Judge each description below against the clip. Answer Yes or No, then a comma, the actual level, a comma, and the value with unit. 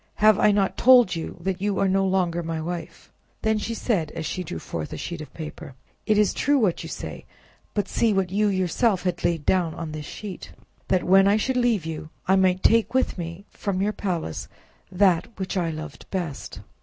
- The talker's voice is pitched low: No, medium, 185 Hz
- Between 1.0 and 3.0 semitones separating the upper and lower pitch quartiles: No, average, 3.6 semitones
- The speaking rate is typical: No, fast, 210 wpm